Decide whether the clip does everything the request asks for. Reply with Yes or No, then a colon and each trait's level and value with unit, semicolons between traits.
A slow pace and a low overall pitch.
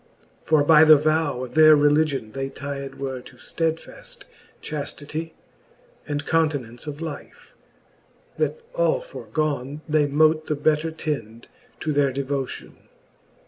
No: slow, 125 wpm; medium, 150 Hz